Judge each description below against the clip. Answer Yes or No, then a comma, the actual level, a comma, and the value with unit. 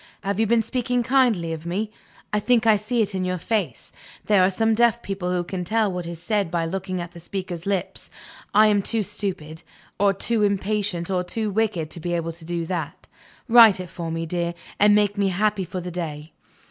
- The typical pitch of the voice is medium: No, high, 195 Hz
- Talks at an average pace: No, fast, 215 wpm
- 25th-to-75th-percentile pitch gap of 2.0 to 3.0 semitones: No, average, 3.6 semitones